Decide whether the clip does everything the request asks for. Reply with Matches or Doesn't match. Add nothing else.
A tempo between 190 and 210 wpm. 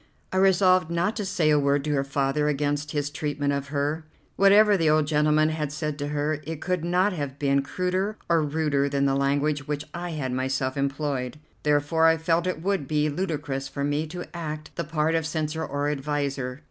Matches